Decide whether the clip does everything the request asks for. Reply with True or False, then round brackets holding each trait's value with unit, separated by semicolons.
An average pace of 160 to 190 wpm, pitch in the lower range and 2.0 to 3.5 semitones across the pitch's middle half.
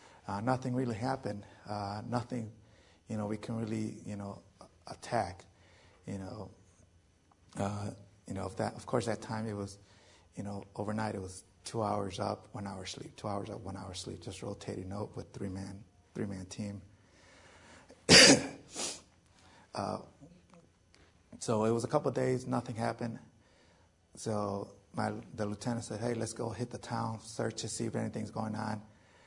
True (170 wpm; 105 Hz; 2.9 semitones)